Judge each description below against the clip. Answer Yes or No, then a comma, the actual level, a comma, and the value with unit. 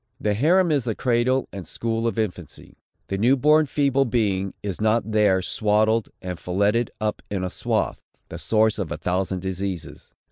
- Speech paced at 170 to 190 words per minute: Yes, average, 175 wpm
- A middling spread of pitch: Yes, average, 3.7 semitones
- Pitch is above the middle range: No, low, 110 Hz